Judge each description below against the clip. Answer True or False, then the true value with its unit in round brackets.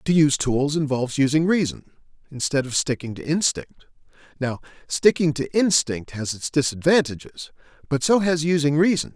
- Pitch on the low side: False (150 Hz)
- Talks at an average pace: True (150 wpm)